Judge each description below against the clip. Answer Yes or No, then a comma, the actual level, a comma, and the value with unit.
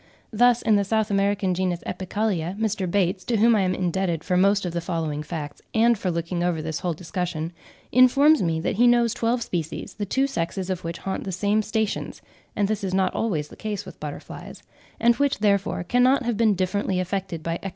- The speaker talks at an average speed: No, fast, 215 wpm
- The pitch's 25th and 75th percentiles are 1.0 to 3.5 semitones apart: No, average, 3.9 semitones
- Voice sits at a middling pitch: No, high, 195 Hz